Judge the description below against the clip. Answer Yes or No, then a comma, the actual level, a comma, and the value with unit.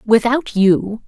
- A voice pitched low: No, high, 225 Hz